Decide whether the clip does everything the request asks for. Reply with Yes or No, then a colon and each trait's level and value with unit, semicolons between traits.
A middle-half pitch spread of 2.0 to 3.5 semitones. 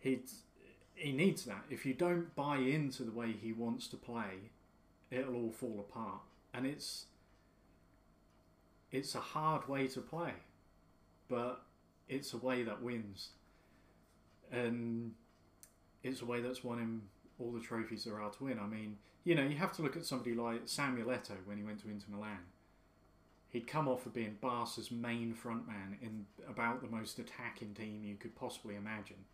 No: average, 3.9 semitones